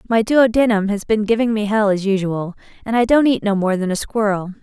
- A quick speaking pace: Yes, fast, 245 wpm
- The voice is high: Yes, high, 210 Hz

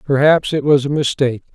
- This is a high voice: No, medium, 140 Hz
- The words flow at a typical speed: Yes, average, 195 wpm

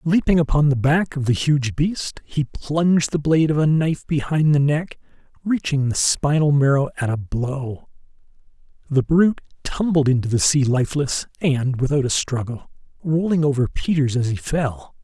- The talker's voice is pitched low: No, medium, 145 Hz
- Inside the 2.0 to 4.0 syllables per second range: No, 4.8 syllables/s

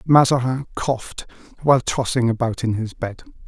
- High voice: No, low, 125 Hz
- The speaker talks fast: No, average, 140 wpm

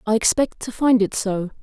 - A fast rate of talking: Yes, fast, 220 wpm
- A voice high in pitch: Yes, high, 220 Hz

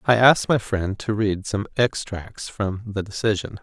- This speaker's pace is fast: No, average, 180 wpm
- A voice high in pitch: No, low, 105 Hz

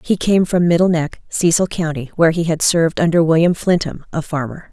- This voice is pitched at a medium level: Yes, medium, 165 Hz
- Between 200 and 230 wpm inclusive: Yes, fast, 205 wpm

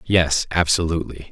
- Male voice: Yes, male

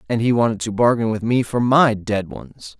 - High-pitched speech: No, low, 110 Hz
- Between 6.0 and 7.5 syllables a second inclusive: No, 5.0 syllables/s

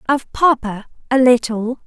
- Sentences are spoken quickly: No, slow, 95 wpm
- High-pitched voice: Yes, high, 245 Hz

